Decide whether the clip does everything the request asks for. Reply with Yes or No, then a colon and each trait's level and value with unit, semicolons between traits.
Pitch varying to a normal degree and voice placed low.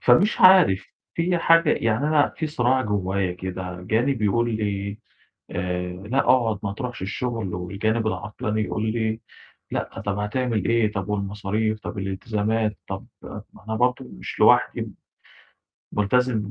Yes: average, 3.8 semitones; low, 110 Hz